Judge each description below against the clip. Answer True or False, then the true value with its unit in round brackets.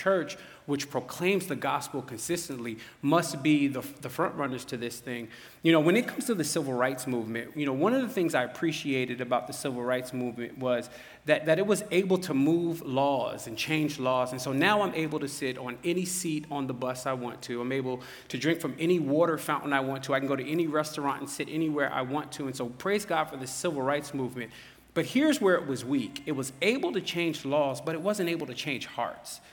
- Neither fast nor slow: False (240 wpm)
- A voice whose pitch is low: False (145 Hz)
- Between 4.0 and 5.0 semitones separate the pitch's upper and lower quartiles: True (4.3 semitones)